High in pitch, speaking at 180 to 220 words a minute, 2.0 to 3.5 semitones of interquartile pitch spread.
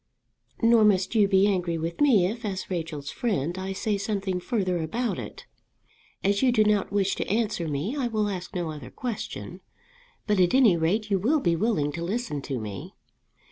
No: high, 195 Hz; average, 190 wpm; average, 4.3 semitones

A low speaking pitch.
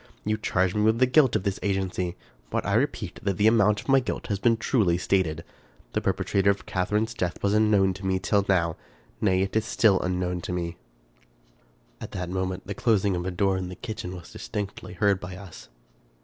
Yes: very low, 95 Hz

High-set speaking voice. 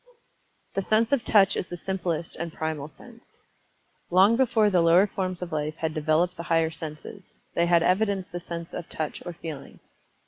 No: medium, 175 Hz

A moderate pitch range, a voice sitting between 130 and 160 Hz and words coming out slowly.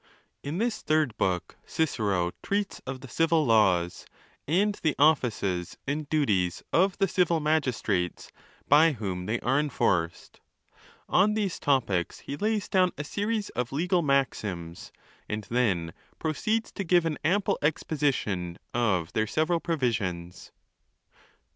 No: wide, 8.8 semitones; medium, 140 Hz; slow, 130 wpm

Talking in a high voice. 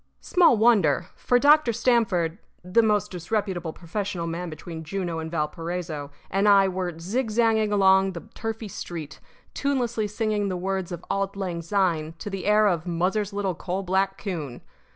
Yes: high, 195 Hz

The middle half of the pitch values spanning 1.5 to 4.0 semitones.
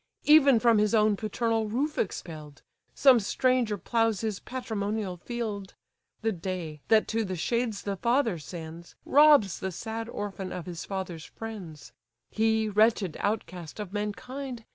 Yes: average, 3.7 semitones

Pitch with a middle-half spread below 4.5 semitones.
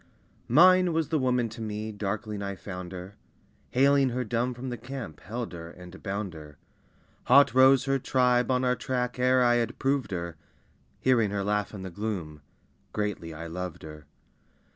No: average, 5.2 semitones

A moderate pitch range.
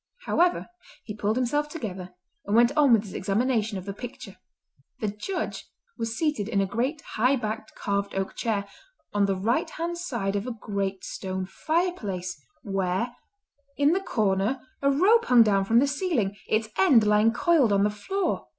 No: wide, 5.8 semitones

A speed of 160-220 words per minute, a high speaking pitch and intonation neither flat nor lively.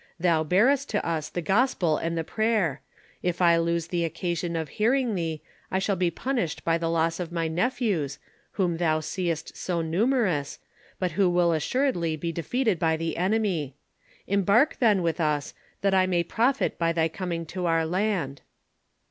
No: average, 175 wpm; medium, 170 Hz; average, 3.4 semitones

